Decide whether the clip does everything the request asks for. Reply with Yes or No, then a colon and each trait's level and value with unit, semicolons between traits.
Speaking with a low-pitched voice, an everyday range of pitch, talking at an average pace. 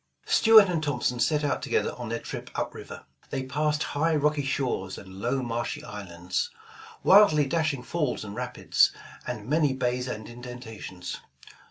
Yes: low, 130 Hz; average, 4.3 semitones; average, 155 wpm